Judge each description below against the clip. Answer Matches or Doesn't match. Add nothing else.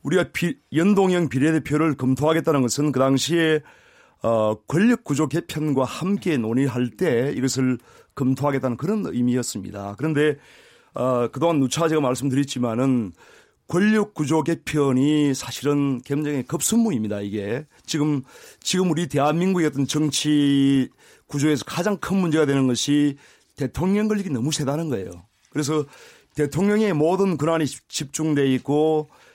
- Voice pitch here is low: Doesn't match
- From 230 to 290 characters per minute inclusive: Doesn't match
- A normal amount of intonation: Matches